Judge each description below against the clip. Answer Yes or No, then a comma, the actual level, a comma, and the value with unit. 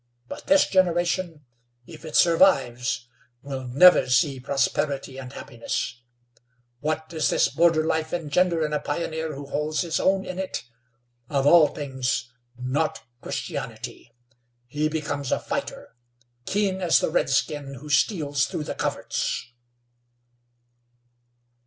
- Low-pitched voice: No, medium, 150 Hz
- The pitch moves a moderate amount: Yes, average, 3.7 semitones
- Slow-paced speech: Yes, slow, 125 wpm